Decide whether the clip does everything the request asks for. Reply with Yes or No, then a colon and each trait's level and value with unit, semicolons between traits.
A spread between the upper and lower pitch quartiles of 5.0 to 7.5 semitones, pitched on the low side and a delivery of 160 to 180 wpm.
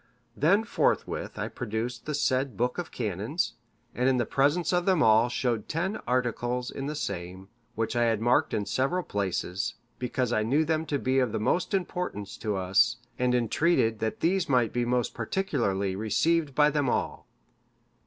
Yes: wide, 5.4 semitones; low, 125 Hz; average, 175 wpm